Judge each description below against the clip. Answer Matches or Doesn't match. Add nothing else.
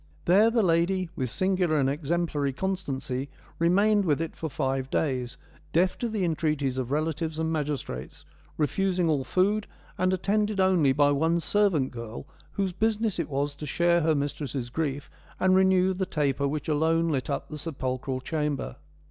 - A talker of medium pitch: Matches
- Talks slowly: Doesn't match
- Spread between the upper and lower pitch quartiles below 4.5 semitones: Doesn't match